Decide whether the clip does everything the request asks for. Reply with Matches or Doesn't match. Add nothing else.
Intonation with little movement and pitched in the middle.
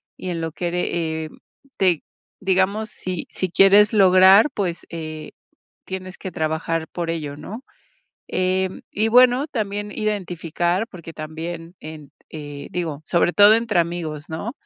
Doesn't match